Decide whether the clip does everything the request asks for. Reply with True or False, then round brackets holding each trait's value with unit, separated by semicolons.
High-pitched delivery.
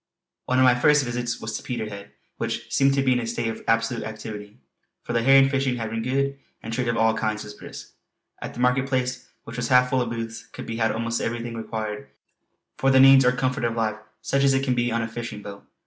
False (120 Hz)